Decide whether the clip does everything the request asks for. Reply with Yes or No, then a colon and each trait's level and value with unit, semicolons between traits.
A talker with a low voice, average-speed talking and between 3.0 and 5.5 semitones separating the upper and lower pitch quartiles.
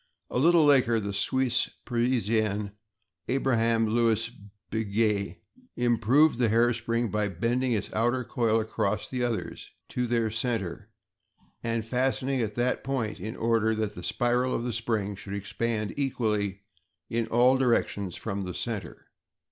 No: low, 115 Hz; average, 145 wpm; narrow, 2.4 semitones